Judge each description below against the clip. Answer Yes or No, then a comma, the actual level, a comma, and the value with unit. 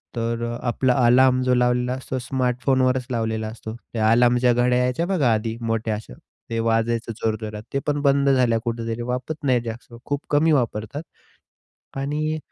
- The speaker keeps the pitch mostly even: Yes, narrow, 2.3 semitones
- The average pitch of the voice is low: Yes, low, 125 Hz